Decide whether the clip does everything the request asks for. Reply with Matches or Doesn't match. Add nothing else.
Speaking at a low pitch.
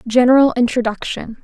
Doesn't match